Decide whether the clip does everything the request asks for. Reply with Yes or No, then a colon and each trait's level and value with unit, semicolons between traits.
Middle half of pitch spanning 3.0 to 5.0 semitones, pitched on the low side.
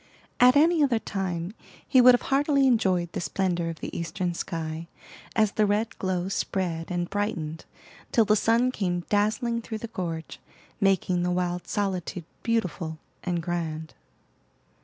No: average, 4.4 semitones; high, 190 Hz